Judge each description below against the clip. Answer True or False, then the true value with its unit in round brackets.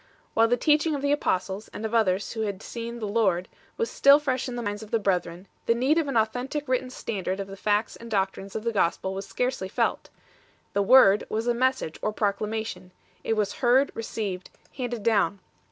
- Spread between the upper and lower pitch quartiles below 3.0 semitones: False (3.9 semitones)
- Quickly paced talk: True (215 wpm)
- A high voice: True (220 Hz)